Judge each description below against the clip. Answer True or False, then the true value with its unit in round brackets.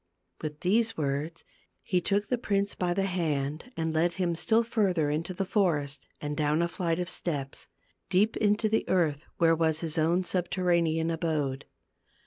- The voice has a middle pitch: True (170 Hz)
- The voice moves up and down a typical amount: True (3.4 semitones)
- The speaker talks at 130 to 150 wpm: False (165 wpm)